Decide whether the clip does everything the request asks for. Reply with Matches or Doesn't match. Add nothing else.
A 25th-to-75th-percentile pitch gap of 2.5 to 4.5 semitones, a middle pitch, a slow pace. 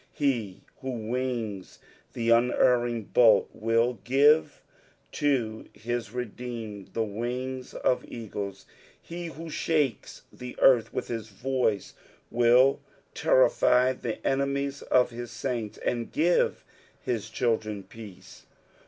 Doesn't match